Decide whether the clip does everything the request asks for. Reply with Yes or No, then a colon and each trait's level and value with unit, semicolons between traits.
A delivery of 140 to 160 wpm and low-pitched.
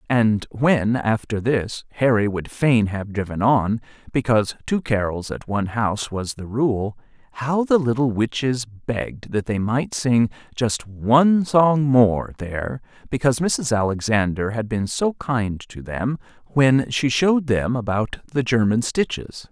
Yes: average, 155 wpm; low, 120 Hz